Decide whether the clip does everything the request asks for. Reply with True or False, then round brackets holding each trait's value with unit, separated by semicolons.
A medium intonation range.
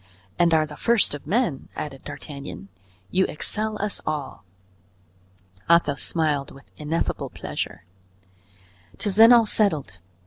False (6.4 semitones)